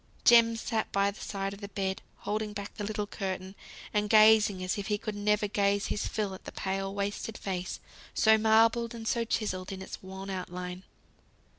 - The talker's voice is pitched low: No, high, 205 Hz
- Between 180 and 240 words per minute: Yes, average, 190 wpm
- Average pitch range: No, narrow, 2.0 semitones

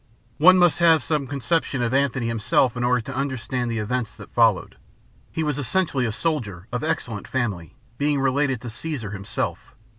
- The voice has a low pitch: Yes, low, 130 Hz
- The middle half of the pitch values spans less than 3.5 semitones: No, average, 4.1 semitones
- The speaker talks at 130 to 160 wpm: No, average, 175 wpm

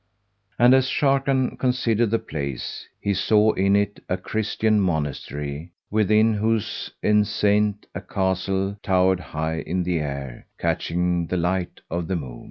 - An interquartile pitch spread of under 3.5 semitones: No, average, 3.9 semitones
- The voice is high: No, very low, 95 Hz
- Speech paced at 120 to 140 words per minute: Yes, slow, 135 wpm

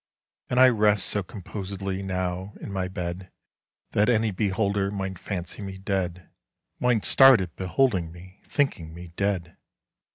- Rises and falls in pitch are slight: Yes, narrow, 2.2 semitones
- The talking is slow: Yes, slow, 110 wpm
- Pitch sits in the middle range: No, very low, 95 Hz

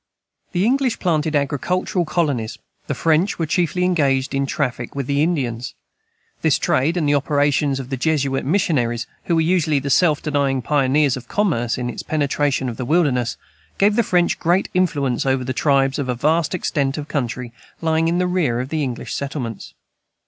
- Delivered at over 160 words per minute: Yes, average, 180 wpm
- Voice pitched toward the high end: No, medium, 145 Hz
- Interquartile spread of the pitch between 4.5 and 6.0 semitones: No, average, 4.0 semitones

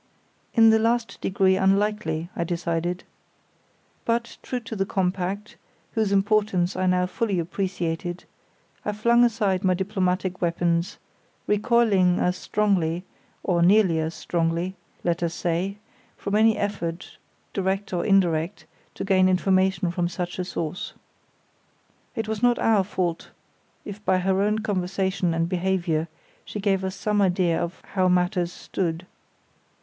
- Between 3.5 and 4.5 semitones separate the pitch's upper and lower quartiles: No, average, 2.8 semitones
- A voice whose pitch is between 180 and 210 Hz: Yes, medium, 185 Hz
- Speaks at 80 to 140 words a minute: Yes, slow, 135 wpm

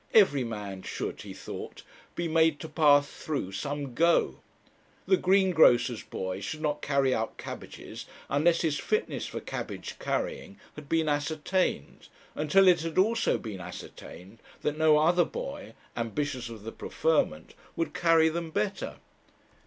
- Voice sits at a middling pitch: Yes, medium, 155 Hz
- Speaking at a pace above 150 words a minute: No, average, 145 wpm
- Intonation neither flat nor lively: Yes, average, 4.9 semitones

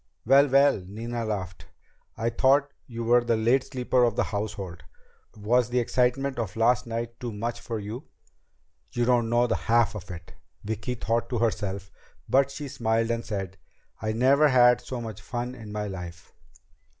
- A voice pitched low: Yes, low, 115 Hz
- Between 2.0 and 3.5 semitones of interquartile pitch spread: Yes, average, 2.8 semitones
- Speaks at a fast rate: No, average, 175 wpm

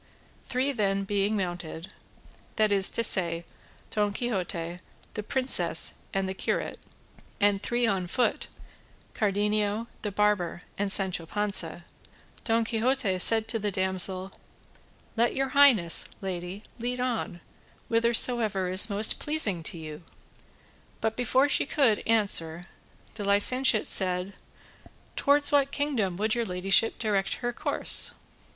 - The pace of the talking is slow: Yes, slow, 125 wpm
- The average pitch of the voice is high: Yes, high, 205 Hz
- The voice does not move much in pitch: No, average, 3.7 semitones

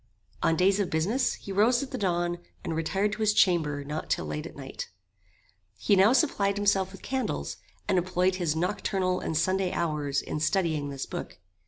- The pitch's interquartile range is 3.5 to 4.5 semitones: Yes, average, 4.0 semitones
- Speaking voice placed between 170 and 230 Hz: Yes, medium, 185 Hz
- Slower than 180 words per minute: No, average, 185 wpm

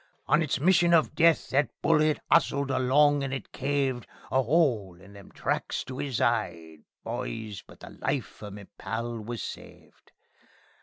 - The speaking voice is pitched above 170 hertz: No, low, 130 Hz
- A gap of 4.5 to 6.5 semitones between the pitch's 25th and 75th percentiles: Yes, average, 5.1 semitones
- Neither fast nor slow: Yes, average, 160 wpm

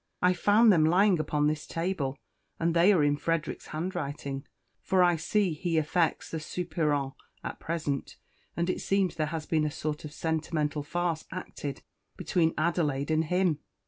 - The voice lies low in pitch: No, medium, 160 Hz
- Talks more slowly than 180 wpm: Yes, average, 170 wpm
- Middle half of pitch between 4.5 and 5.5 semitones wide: No, average, 2.8 semitones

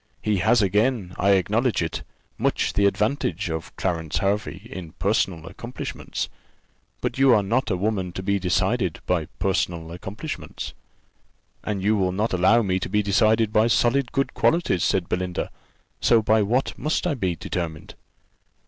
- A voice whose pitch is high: No, low, 100 Hz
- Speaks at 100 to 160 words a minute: Yes, average, 155 wpm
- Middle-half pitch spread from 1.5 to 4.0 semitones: Yes, average, 3.5 semitones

